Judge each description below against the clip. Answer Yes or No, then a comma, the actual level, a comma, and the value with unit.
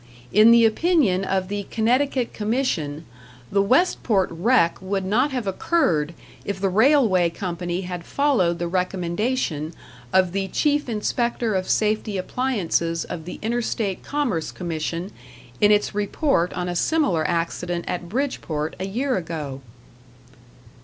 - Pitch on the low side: No, high, 195 Hz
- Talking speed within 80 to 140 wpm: Yes, slow, 135 wpm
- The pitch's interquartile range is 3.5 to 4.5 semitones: No, wide, 5.5 semitones